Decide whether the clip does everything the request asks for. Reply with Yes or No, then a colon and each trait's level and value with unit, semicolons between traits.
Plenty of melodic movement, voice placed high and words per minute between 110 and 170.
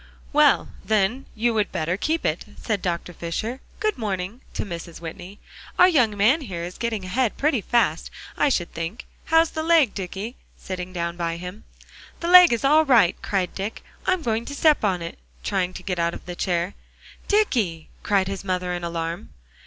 No: wide, 6.2 semitones; high, 200 Hz; average, 185 wpm